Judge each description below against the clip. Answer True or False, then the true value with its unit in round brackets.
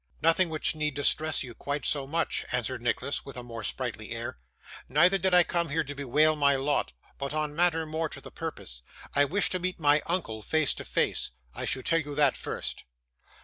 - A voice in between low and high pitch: True (150 Hz)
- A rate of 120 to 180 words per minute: False (205 wpm)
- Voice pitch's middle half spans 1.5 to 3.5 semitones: True (3.1 semitones)